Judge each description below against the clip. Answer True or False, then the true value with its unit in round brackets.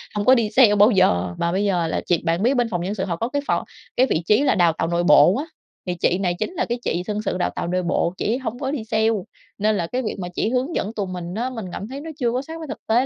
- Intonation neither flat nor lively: False (5.8 semitones)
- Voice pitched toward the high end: True (210 Hz)